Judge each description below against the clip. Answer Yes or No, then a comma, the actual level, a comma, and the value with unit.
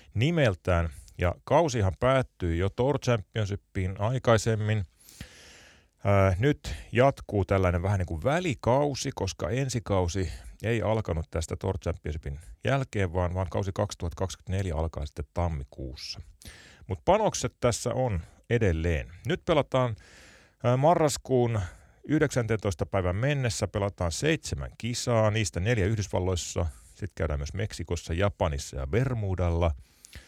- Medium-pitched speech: No, low, 100 Hz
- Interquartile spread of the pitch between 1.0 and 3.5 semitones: No, average, 5.2 semitones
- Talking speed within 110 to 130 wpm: Yes, average, 115 wpm